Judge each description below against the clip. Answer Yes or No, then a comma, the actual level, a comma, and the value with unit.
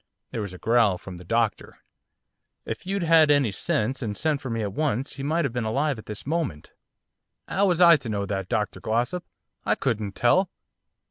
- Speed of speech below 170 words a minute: No, average, 200 wpm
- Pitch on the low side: Yes, low, 120 Hz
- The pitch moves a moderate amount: No, wide, 6.7 semitones